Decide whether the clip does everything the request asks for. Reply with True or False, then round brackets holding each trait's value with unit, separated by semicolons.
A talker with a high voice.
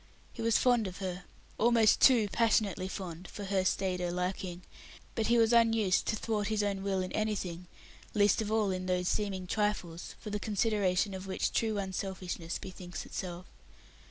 True (195 Hz)